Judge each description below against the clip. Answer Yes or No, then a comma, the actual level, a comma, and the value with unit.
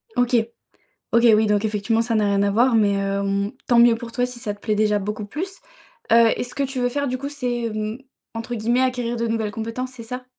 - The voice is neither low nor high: No, high, 230 Hz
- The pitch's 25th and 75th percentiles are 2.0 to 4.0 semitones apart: Yes, average, 2.8 semitones